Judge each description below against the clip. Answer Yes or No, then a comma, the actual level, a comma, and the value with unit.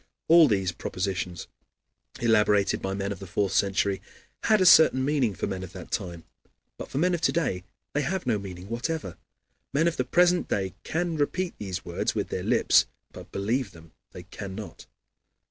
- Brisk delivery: No, average, 180 wpm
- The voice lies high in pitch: No, low, 105 Hz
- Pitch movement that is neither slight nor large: No, wide, 8.5 semitones